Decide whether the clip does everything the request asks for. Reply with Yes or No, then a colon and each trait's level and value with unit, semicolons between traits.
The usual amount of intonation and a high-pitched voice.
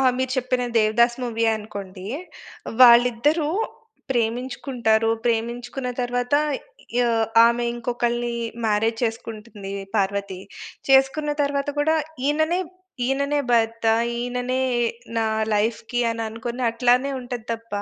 No: narrow, 2.3 semitones; high, 240 Hz